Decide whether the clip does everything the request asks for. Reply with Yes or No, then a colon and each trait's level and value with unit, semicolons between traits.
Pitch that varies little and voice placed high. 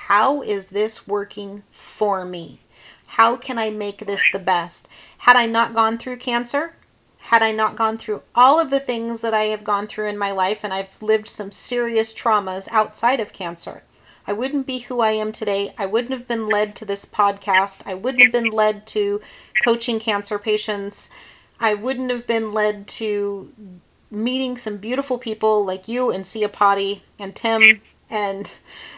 Yes: narrow, 2.3 semitones; high, 215 Hz